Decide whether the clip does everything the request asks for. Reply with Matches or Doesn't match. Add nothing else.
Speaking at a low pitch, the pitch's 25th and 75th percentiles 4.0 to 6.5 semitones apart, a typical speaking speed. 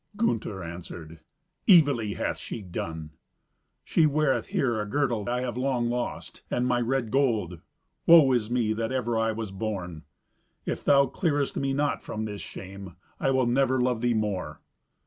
Matches